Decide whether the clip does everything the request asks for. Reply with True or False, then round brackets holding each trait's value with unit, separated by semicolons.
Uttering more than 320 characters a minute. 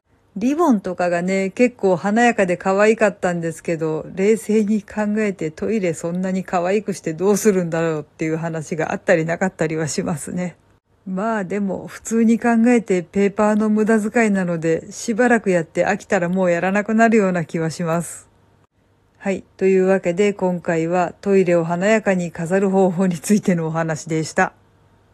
True (360 characters per minute)